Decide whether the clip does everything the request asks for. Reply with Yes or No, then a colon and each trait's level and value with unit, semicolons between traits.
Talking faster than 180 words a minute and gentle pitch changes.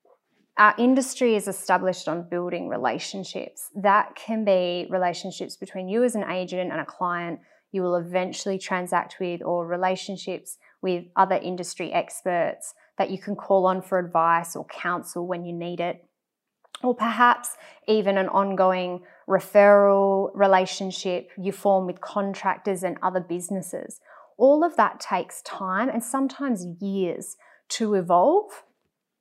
No: average, 140 wpm; narrow, 2.2 semitones